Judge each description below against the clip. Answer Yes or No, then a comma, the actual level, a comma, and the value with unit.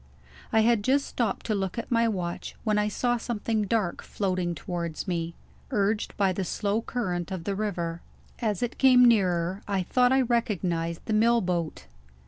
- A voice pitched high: Yes, high, 205 Hz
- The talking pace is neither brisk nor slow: Yes, average, 175 wpm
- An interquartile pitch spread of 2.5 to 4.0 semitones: No, average, 4.6 semitones